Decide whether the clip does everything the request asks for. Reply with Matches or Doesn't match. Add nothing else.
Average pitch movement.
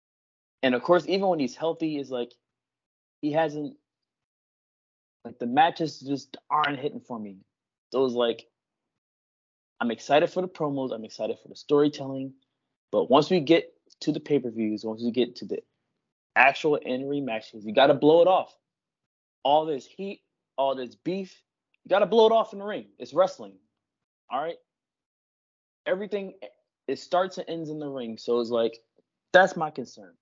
Doesn't match